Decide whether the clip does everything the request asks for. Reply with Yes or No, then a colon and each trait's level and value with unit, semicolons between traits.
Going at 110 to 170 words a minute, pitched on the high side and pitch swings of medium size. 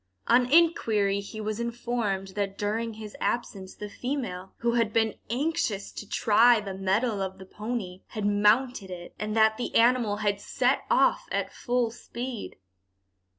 Yes: average, 155 wpm; high, 215 Hz; average, 3.1 semitones